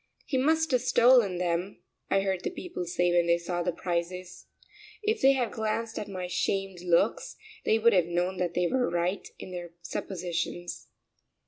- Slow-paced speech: No, average, 180 wpm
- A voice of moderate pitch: Yes, medium, 180 Hz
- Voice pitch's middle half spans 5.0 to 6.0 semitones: No, average, 4.2 semitones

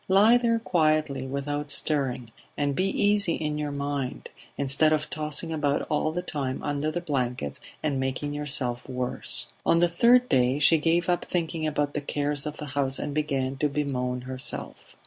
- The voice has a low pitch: No, medium, 145 Hz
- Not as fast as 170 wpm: No, average, 175 wpm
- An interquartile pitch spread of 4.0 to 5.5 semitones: No, average, 2.7 semitones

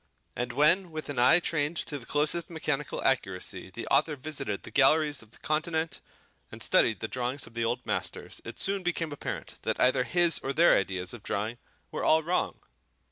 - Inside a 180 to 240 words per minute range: Yes, average, 190 wpm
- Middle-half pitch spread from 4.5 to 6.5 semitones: Yes, average, 4.9 semitones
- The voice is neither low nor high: Yes, medium, 145 Hz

